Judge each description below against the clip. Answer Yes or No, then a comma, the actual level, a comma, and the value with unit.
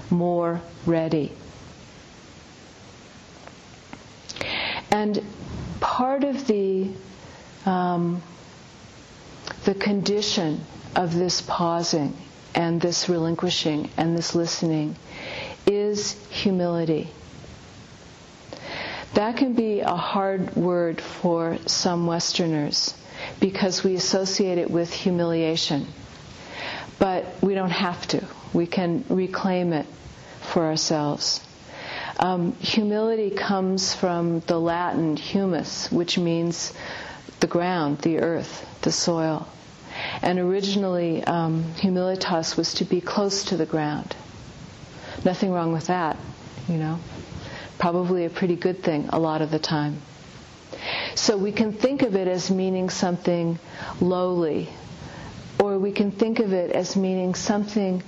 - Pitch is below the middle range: No, medium, 175 Hz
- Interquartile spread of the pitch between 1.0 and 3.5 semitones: Yes, narrow, 2.6 semitones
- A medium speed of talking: No, slow, 110 wpm